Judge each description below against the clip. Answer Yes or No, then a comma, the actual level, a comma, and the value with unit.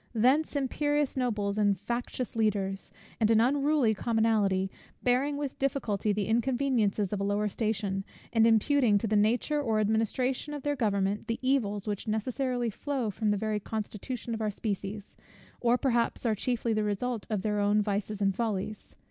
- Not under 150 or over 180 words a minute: Yes, average, 170 wpm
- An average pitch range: Yes, average, 3.3 semitones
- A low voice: No, high, 220 Hz